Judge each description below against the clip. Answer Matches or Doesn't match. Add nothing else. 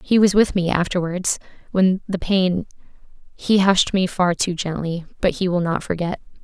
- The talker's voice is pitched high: Doesn't match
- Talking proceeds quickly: Doesn't match